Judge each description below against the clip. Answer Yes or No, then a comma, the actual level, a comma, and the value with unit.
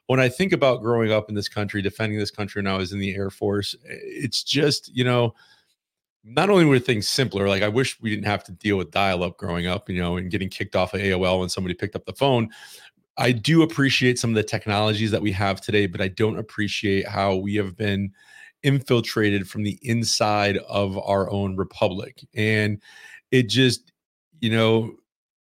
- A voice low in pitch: Yes, low, 105 Hz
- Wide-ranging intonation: No, average, 3.5 semitones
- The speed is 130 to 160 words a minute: No, fast, 205 wpm